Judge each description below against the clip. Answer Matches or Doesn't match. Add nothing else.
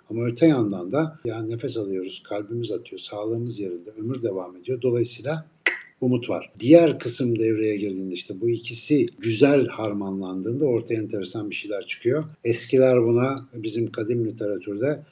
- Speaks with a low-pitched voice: Matches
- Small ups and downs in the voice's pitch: Doesn't match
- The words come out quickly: Matches